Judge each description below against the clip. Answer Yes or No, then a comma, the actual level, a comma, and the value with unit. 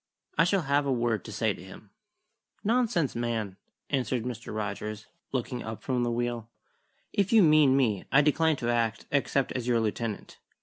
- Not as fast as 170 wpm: No, average, 175 wpm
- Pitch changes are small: No, average, 4.1 semitones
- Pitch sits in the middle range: No, low, 125 Hz